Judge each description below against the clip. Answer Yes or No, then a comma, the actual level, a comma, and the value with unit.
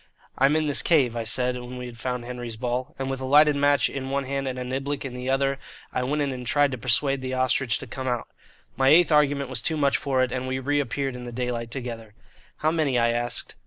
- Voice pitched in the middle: No, low, 130 Hz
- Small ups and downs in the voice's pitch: Yes, narrow, 2.0 semitones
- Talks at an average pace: No, fast, 250 wpm